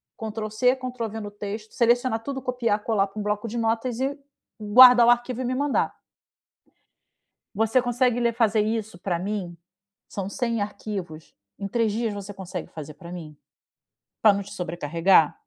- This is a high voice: Yes, high, 215 Hz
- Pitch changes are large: No, average, 3.4 semitones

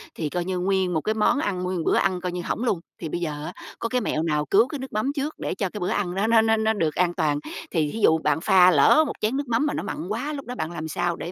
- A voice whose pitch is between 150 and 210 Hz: Yes, medium, 185 Hz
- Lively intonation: No, average, 5.0 semitones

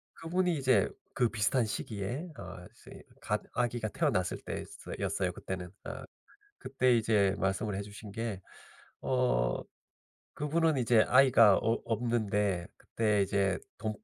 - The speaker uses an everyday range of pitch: Yes, average, 4.0 semitones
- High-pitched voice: No, low, 110 Hz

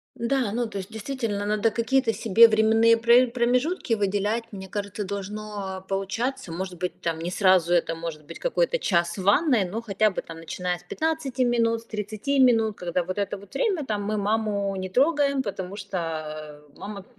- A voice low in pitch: No, high, 210 Hz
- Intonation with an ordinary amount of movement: Yes, average, 3.8 semitones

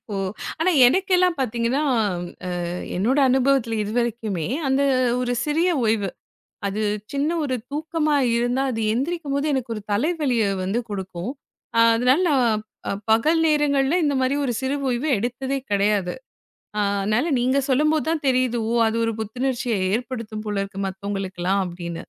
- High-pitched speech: Yes, high, 245 Hz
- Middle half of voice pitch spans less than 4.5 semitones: No, average, 4.8 semitones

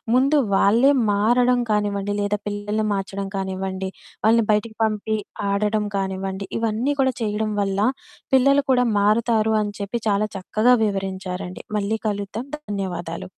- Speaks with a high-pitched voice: Yes, high, 210 Hz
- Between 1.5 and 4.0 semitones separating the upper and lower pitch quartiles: Yes, narrow, 2.6 semitones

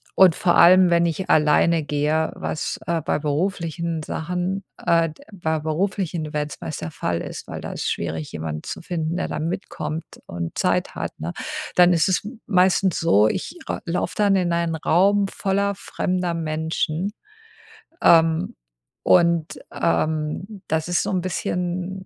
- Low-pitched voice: No, medium, 170 Hz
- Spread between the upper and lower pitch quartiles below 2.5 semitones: No, average, 2.9 semitones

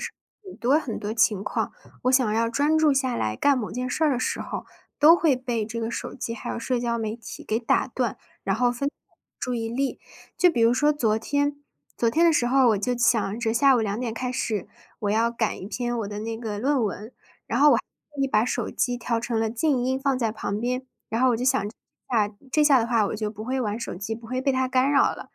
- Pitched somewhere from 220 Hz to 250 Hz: Yes, high, 240 Hz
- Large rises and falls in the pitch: No, average, 2.8 semitones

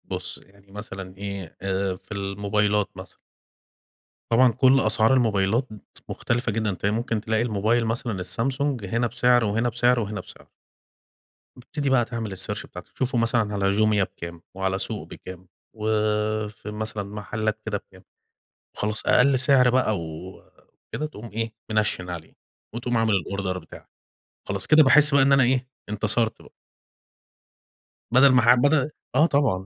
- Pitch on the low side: Yes, low, 110 Hz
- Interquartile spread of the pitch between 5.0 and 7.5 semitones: No, average, 3.5 semitones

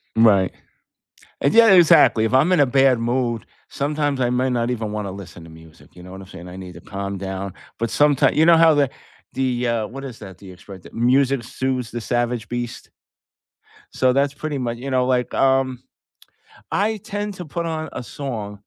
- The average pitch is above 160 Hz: No, low, 125 Hz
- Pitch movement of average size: Yes, average, 4.7 semitones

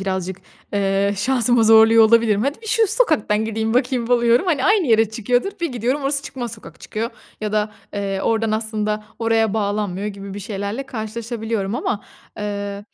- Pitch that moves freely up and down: No, average, 2.9 semitones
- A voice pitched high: Yes, high, 220 Hz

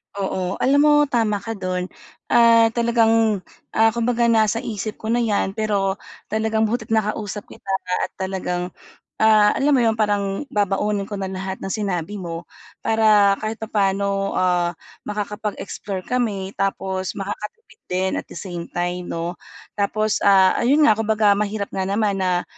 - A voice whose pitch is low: No, high, 205 Hz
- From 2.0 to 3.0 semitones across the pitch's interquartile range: Yes, narrow, 2.5 semitones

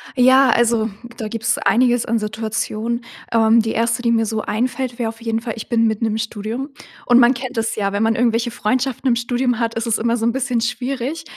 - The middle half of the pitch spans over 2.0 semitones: No, narrow, 1.7 semitones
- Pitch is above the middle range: Yes, high, 230 Hz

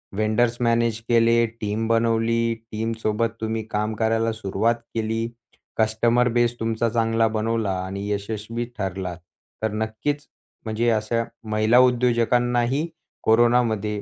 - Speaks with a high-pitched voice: No, low, 115 Hz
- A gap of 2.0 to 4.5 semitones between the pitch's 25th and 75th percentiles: No, narrow, 1.3 semitones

